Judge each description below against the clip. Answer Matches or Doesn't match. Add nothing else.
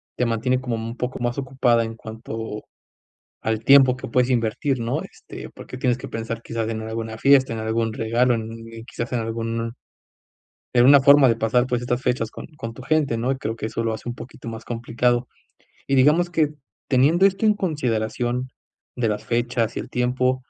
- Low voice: Matches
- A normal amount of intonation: Doesn't match